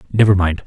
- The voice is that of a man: Yes, male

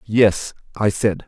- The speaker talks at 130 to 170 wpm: Yes, average, 140 wpm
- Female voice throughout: No, male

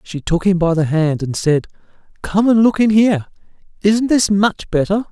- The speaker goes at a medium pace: Yes, average, 190 wpm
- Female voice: No, male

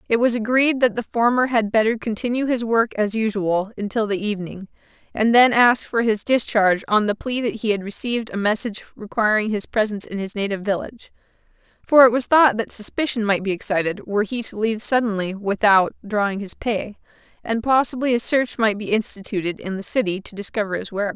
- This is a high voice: Yes, high, 220 Hz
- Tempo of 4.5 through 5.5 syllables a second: No, 5.9 syllables/s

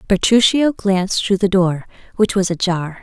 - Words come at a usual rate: Yes, average, 160 wpm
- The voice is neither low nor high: No, high, 195 Hz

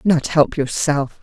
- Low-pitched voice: No, medium, 150 Hz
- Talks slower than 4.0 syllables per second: Yes, 3.5 syllables/s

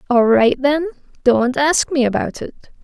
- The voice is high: Yes, very high, 265 Hz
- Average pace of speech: Yes, average, 170 wpm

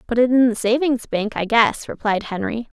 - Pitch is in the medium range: No, high, 230 Hz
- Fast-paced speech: Yes, fast, 215 wpm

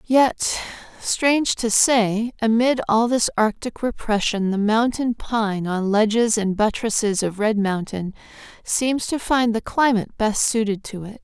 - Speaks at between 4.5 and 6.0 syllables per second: No, 4.1 syllables/s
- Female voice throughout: Yes, female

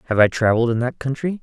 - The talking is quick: Yes, fast, 250 wpm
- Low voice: Yes, low, 125 Hz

